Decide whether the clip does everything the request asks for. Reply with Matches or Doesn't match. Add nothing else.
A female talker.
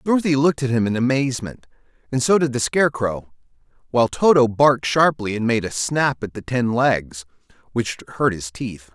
Doesn't match